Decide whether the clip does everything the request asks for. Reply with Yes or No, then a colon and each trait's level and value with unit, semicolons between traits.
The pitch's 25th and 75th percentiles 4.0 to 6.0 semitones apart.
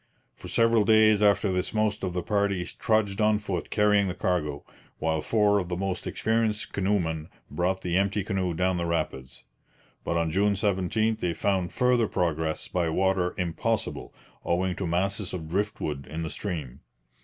No: average, 3.3 semitones